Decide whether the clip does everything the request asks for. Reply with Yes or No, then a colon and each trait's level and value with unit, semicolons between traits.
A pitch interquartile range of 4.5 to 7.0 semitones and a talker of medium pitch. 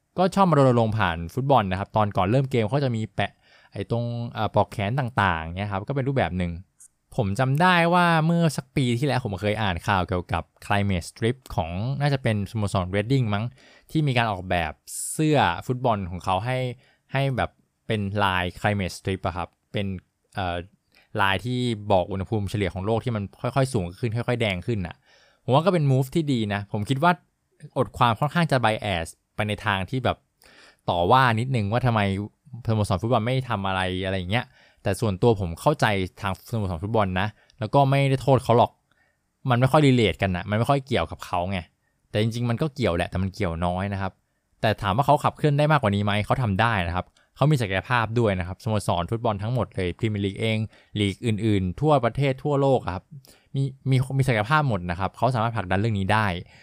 No: average, 5.1 semitones; low, 110 Hz